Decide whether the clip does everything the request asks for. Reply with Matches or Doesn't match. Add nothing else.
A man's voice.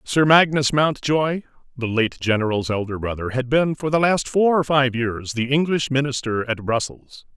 Matches